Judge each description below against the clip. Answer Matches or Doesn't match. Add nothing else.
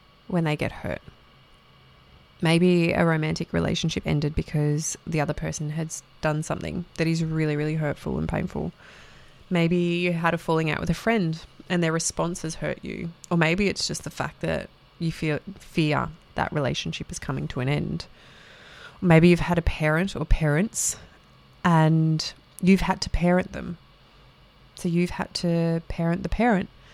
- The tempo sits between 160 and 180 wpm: Matches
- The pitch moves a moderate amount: Doesn't match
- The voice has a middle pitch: Matches